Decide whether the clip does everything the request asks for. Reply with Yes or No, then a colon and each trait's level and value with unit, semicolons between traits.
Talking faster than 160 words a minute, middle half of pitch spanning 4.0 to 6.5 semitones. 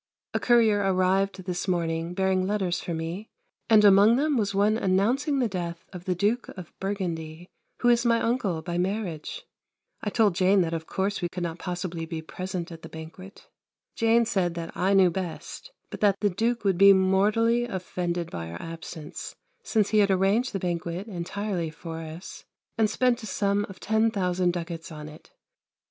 No: average, 180 wpm; average, 3.5 semitones